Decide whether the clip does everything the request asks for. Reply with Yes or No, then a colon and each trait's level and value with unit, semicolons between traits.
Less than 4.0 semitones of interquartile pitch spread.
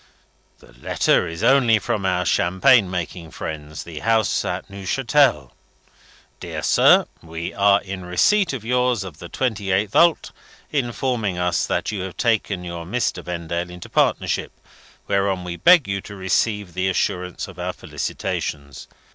No: average, 4.4 semitones